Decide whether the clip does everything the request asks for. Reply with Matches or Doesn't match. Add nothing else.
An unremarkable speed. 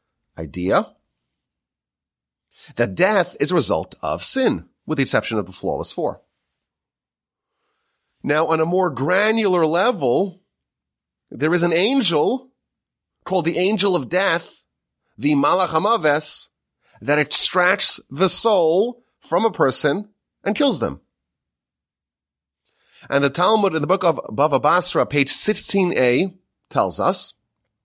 Doesn't match